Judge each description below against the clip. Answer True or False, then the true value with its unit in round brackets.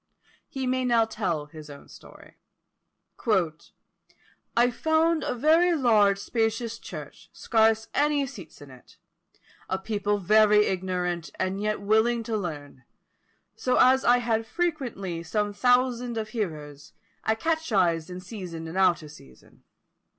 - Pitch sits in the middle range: False (215 Hz)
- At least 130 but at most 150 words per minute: True (135 wpm)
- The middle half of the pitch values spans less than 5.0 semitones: False (5.4 semitones)